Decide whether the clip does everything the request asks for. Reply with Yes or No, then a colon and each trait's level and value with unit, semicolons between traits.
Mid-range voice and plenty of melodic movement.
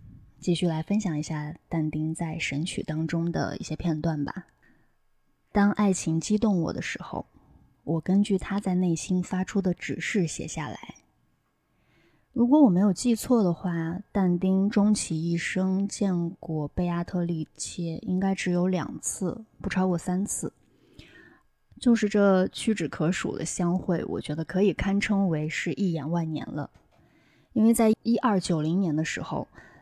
No: medium, 180 Hz; average, 3.5 semitones